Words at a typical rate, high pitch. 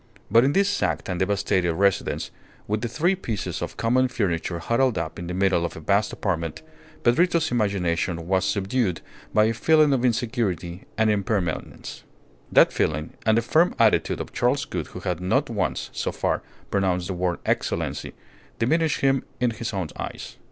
No: average, 175 wpm; low, 105 Hz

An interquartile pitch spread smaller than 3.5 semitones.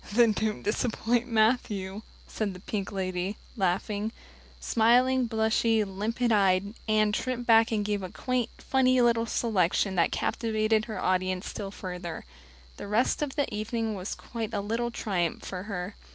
Yes: average, 3.0 semitones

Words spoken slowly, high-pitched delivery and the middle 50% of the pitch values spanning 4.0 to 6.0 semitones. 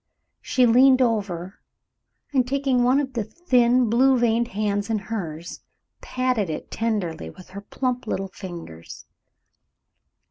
Yes: slow, 130 wpm; high, 225 Hz; average, 4.6 semitones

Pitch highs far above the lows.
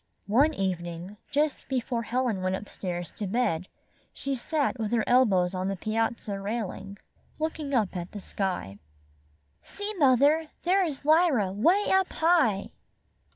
Yes: wide, 7.3 semitones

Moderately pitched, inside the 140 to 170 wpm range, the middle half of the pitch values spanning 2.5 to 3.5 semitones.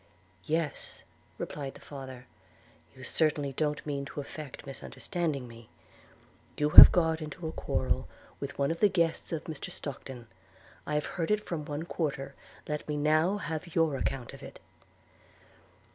Yes: medium, 150 Hz; average, 160 wpm; average, 2.8 semitones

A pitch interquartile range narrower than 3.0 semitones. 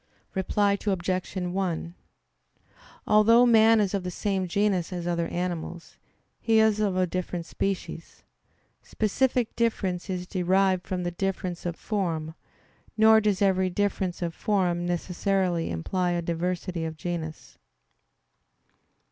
Yes: narrow, 2.6 semitones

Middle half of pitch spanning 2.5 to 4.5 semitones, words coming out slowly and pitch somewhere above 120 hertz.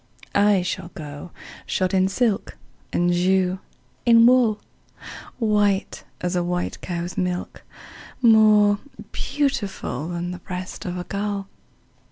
Yes: average, 2.9 semitones; slow, 120 wpm; high, 190 Hz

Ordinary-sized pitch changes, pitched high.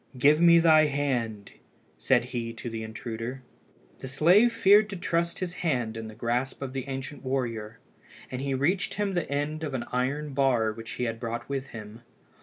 No: average, 5.0 semitones; low, 135 Hz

